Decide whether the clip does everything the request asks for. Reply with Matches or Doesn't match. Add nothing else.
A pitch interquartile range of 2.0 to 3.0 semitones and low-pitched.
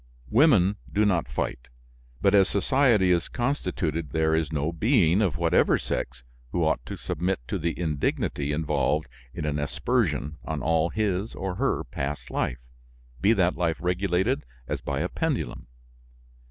Doesn't match